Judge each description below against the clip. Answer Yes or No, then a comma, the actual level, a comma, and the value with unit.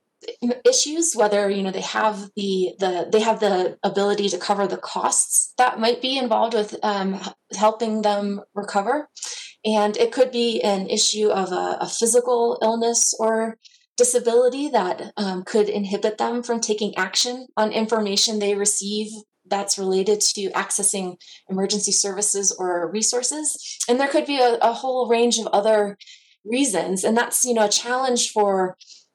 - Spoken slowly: No, average, 155 wpm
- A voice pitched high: Yes, high, 215 Hz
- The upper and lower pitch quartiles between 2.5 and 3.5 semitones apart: Yes, average, 3.0 semitones